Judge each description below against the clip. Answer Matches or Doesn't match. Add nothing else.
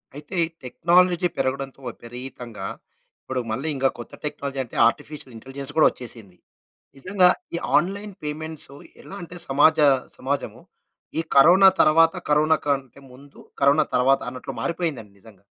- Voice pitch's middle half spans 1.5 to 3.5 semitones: Doesn't match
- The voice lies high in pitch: Doesn't match